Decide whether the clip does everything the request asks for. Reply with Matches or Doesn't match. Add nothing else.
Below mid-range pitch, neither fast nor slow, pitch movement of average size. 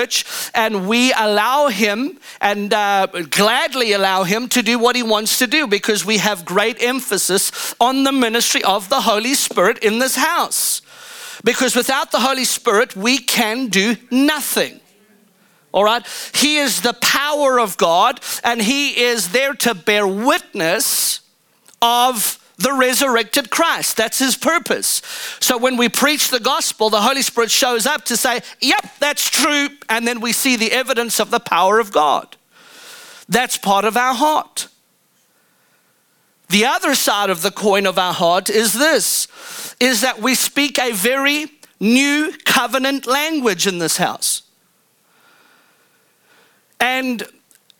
Doesn't match